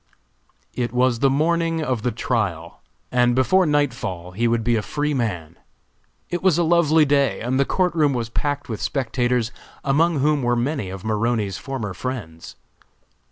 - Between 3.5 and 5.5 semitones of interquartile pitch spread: Yes, average, 4.6 semitones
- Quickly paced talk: No, average, 165 wpm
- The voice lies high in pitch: No, low, 125 Hz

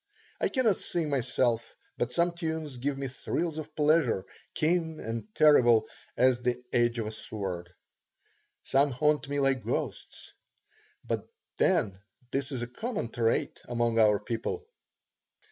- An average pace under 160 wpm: Yes, average, 140 wpm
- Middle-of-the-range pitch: No, low, 130 Hz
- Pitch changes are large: No, average, 4.7 semitones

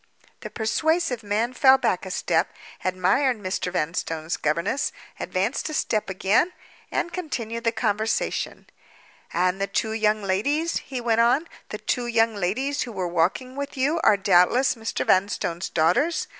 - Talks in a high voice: Yes, high, 225 Hz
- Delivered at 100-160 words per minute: Yes, average, 140 wpm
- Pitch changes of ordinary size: No, wide, 5.8 semitones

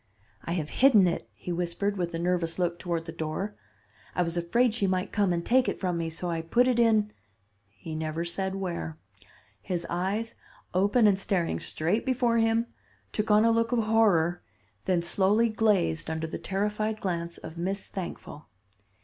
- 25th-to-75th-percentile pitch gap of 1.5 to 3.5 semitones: No, average, 4.0 semitones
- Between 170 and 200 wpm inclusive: Yes, average, 185 wpm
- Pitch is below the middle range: No, medium, 185 Hz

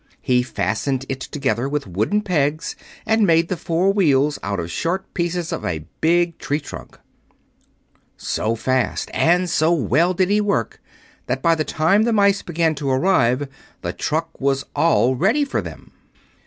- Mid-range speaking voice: Yes, medium, 155 Hz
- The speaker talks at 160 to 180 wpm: Yes, average, 165 wpm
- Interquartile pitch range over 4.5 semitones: Yes, average, 5.2 semitones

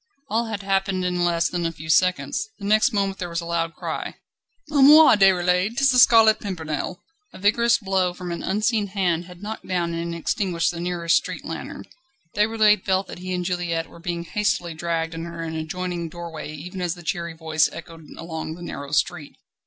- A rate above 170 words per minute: Yes, average, 195 wpm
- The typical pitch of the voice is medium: Yes, medium, 175 Hz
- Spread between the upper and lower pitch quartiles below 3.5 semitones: Yes, average, 2.9 semitones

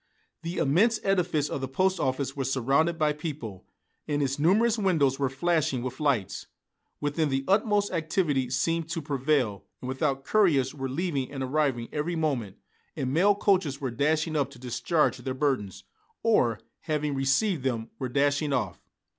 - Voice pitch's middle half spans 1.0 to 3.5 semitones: No, average, 3.9 semitones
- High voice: No, medium, 145 Hz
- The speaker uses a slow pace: No, average, 165 wpm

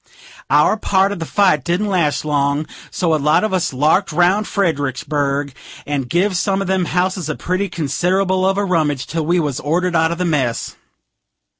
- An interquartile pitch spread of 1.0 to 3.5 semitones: No, average, 4.2 semitones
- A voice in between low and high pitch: Yes, medium, 170 Hz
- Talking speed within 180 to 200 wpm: Yes, average, 185 wpm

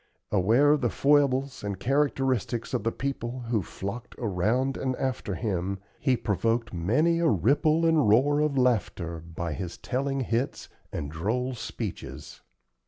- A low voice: Yes, low, 120 Hz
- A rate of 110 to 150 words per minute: Yes, average, 145 wpm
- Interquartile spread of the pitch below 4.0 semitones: No, wide, 5.6 semitones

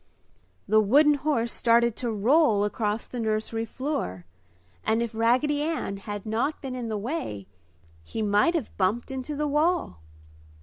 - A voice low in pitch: No, high, 230 Hz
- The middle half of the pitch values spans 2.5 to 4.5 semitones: No, wide, 5.4 semitones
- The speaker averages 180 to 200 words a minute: No, average, 150 wpm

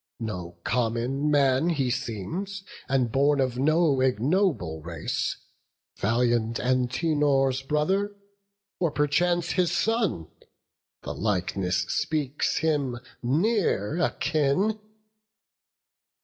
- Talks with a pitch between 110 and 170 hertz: Yes, low, 135 Hz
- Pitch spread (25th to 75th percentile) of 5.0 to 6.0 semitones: Yes, wide, 5.4 semitones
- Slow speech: Yes, slow, 90 wpm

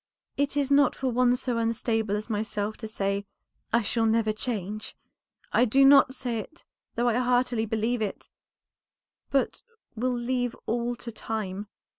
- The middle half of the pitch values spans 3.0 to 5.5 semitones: No, narrow, 2.5 semitones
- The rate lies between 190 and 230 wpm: No, average, 155 wpm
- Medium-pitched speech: No, high, 235 Hz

